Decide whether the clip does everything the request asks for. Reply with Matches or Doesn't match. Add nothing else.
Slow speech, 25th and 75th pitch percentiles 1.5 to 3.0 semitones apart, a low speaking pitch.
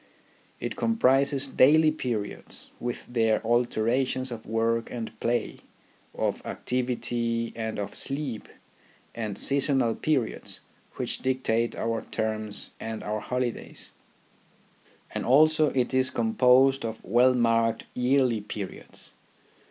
Matches